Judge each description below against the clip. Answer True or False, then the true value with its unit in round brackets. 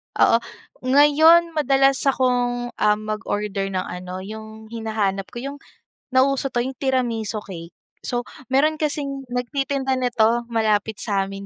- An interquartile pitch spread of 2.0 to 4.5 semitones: True (4.2 semitones)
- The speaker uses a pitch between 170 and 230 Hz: False (245 Hz)